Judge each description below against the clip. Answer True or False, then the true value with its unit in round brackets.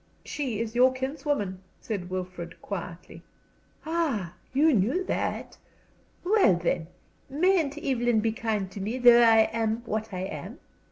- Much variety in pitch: True (5.8 semitones)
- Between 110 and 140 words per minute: True (135 wpm)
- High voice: True (230 Hz)